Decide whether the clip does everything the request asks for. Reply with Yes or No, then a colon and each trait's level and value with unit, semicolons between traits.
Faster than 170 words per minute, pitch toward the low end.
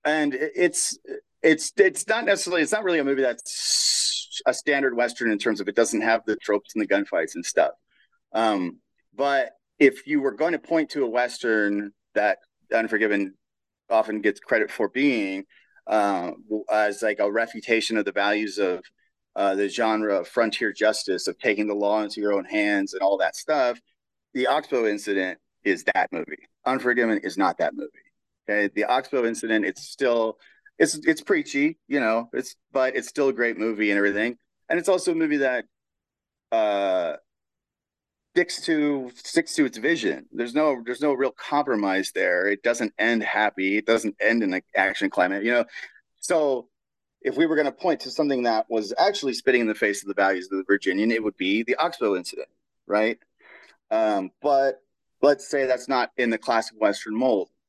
Yes: average, 185 wpm; low, 125 Hz